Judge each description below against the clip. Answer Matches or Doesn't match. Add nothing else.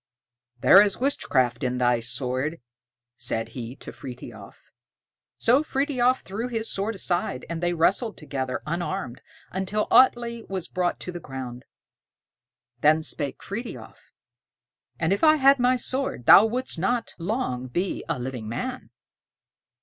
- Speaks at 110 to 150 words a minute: Matches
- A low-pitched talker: Doesn't match